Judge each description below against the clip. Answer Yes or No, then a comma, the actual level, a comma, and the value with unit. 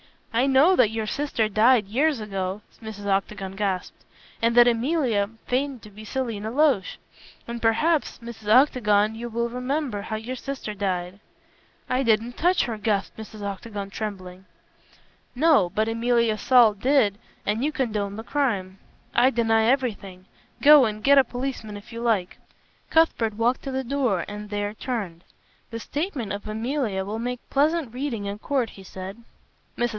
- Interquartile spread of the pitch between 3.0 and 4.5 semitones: Yes, average, 3.9 semitones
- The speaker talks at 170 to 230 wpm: No, average, 160 wpm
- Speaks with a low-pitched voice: No, high, 225 Hz